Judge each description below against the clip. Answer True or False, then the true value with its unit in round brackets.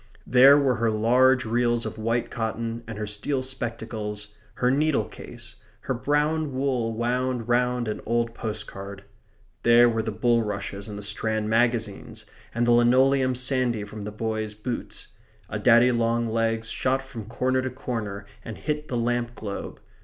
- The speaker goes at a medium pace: True (160 wpm)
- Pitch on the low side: True (120 Hz)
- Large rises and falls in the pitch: False (2.5 semitones)